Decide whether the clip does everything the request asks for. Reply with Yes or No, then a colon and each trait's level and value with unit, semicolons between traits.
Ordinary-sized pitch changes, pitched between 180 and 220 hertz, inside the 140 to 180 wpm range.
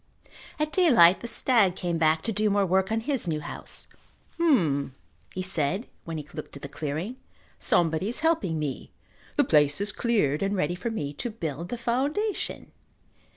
No: wide, 7.0 semitones; high, 190 Hz; average, 175 wpm